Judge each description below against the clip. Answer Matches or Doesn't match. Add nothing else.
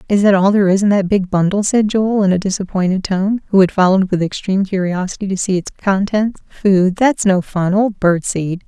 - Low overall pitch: Doesn't match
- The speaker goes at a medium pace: Doesn't match